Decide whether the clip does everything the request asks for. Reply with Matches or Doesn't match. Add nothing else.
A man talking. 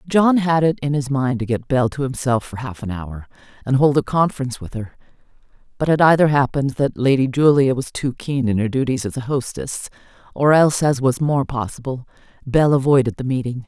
Doesn't match